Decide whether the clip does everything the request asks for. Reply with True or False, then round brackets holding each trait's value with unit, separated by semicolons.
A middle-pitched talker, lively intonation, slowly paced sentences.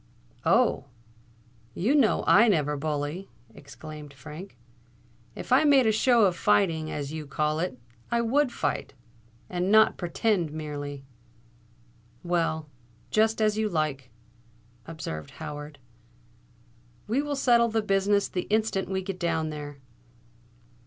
True (170 Hz; 6.5 semitones; 120 wpm)